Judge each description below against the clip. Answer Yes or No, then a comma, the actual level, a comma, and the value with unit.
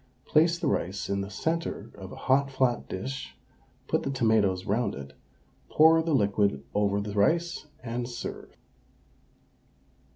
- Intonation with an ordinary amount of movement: No, wide, 5.7 semitones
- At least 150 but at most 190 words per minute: No, average, 140 wpm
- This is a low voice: Yes, low, 115 Hz